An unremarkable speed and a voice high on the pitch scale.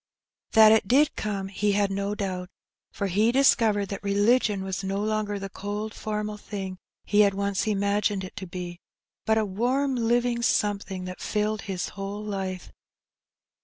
Yes: average, 165 wpm; high, 205 Hz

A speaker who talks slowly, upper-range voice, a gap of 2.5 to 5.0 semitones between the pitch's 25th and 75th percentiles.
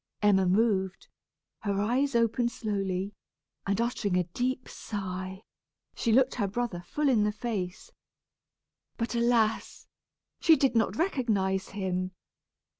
Yes: slow, 120 wpm; high, 210 Hz; average, 4.0 semitones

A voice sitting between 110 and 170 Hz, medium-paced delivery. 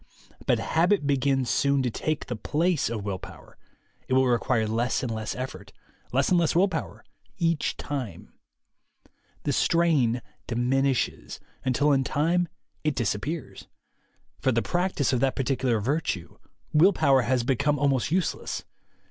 Yes: low, 135 Hz; average, 145 wpm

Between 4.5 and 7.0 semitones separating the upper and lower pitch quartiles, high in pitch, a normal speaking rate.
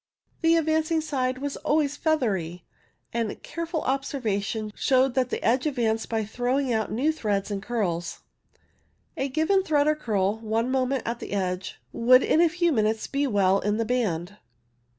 Yes: average, 5.3 semitones; high, 245 Hz; average, 170 wpm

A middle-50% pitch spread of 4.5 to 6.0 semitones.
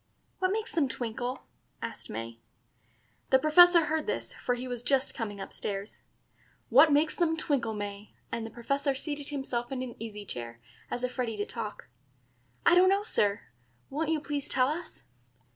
Yes: wide, 5.5 semitones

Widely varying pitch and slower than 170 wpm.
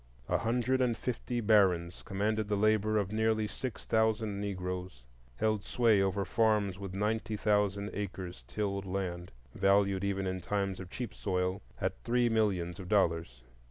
No: average, 2.7 semitones; average, 155 wpm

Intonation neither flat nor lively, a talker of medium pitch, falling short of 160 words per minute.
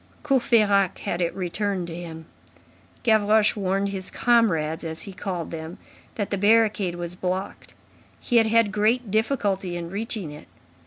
No: average, 3.8 semitones; high, 195 Hz; average, 150 wpm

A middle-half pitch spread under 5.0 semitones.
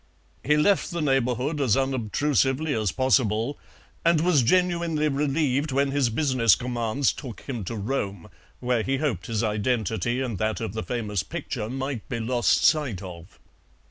Yes: average, 4.5 semitones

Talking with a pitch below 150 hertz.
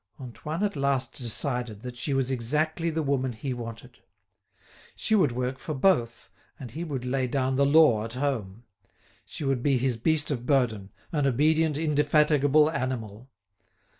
Yes: low, 135 Hz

